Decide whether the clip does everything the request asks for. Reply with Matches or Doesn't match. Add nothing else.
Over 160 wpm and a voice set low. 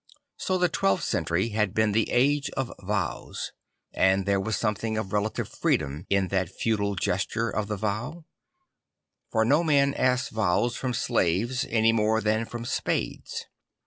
Doesn't match